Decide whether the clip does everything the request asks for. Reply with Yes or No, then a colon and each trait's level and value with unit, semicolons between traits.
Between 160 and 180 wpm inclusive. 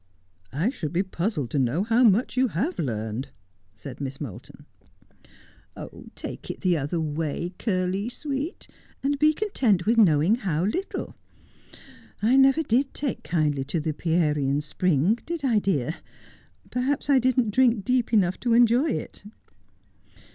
No: average, 150 wpm